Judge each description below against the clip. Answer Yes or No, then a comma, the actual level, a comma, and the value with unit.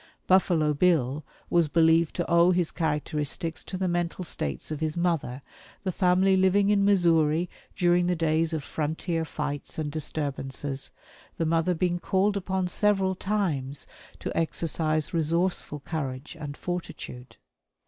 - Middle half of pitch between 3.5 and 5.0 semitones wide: No, average, 3.1 semitones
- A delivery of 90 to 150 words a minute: Yes, average, 140 wpm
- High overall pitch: No, medium, 165 Hz